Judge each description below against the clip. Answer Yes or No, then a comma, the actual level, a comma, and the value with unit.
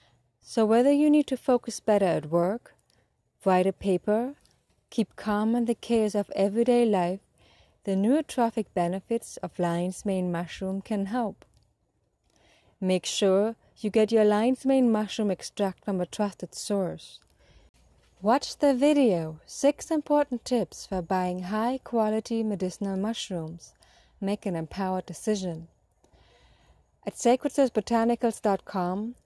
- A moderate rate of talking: No, slow, 125 wpm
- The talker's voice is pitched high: Yes, high, 210 Hz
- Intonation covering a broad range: No, average, 4.3 semitones